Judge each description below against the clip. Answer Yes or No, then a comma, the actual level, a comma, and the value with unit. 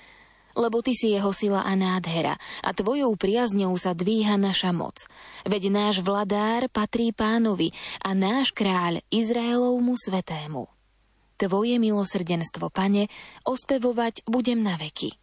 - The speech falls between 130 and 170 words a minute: No, average, 120 wpm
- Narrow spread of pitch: No, average, 3.7 semitones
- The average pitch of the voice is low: No, high, 205 Hz